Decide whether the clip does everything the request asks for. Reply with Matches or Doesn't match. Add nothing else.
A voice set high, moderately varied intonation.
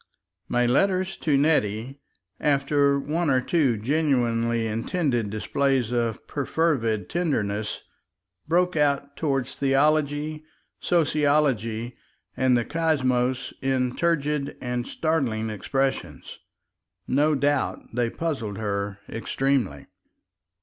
Doesn't match